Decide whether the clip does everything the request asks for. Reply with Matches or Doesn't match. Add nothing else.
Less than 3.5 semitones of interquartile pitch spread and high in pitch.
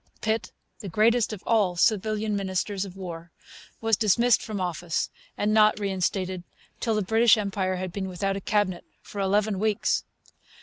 Matches